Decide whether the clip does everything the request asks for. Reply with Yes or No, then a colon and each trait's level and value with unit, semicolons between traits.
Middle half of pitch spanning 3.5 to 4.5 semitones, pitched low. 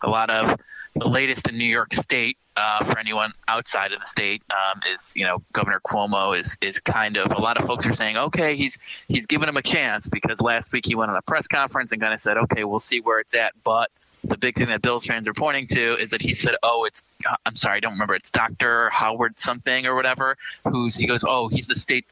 No: average, 2.9 semitones; low, 120 Hz